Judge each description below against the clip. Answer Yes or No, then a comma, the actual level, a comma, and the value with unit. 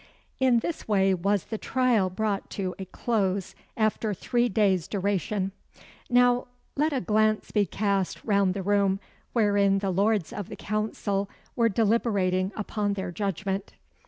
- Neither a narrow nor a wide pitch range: No, narrow, 2.2 semitones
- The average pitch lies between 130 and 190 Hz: No, high, 205 Hz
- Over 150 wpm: No, average, 145 wpm